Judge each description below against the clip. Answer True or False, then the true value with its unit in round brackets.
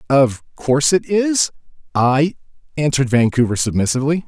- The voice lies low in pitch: False (145 Hz)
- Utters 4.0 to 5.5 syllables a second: True (5.2 syllables/s)